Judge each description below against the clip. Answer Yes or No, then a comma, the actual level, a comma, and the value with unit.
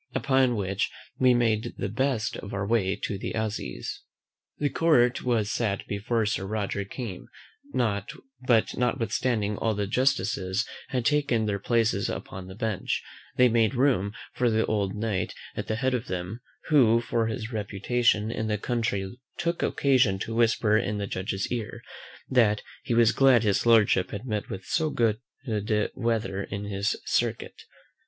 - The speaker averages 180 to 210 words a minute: No, average, 160 wpm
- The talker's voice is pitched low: Yes, low, 110 Hz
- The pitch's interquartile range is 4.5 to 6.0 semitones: No, average, 3.2 semitones